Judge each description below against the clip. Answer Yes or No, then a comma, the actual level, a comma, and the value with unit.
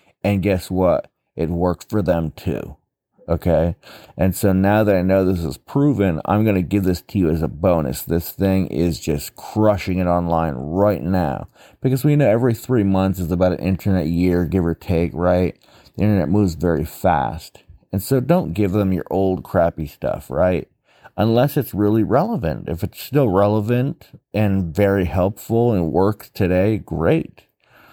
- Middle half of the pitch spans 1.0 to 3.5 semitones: Yes, average, 3.0 semitones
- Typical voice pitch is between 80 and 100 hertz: Yes, very low, 95 Hz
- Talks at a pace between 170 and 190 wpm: Yes, average, 175 wpm